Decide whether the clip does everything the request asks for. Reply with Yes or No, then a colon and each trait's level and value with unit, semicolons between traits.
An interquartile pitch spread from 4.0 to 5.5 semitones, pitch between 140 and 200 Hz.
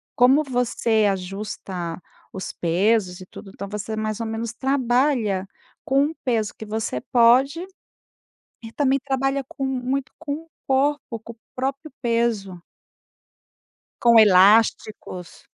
No: average, 4.3 semitones; high, 230 Hz